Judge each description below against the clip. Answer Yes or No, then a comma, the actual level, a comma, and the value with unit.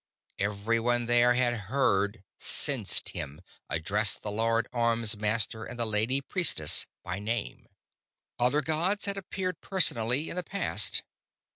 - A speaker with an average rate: No, slow, 125 wpm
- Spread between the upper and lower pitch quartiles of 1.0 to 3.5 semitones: No, average, 4.7 semitones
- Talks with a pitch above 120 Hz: No, low, 115 Hz